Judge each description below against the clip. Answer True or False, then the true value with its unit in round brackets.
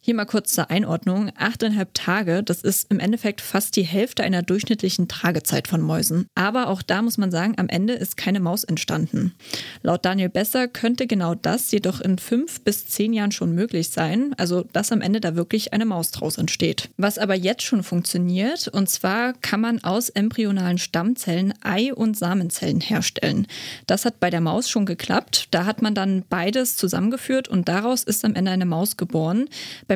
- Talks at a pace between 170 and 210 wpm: True (190 wpm)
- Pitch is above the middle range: True (200 Hz)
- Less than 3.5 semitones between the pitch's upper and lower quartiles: False (3.8 semitones)